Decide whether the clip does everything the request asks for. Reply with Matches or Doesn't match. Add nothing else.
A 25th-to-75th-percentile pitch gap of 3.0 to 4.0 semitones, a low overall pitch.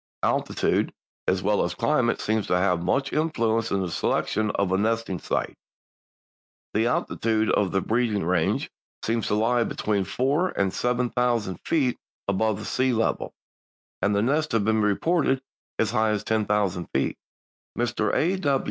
Matches